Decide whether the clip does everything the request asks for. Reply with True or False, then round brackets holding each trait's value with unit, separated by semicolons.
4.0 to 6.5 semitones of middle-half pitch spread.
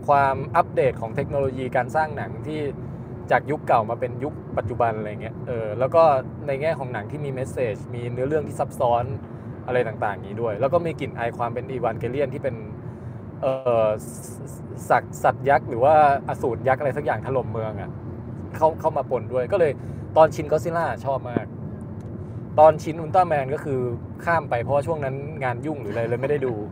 False (3.4 semitones)